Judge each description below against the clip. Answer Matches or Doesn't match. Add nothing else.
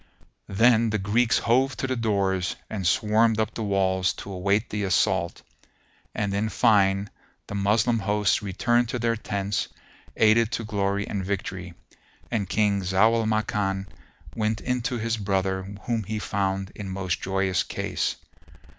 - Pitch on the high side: Doesn't match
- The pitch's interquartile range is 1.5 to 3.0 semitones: Matches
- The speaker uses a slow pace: Doesn't match